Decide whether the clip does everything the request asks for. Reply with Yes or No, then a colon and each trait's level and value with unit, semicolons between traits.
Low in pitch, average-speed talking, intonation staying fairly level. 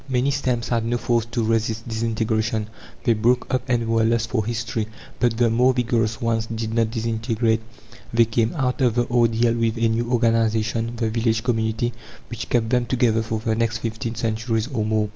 Yes: low, 115 Hz; average, 190 wpm; narrow, 1.3 semitones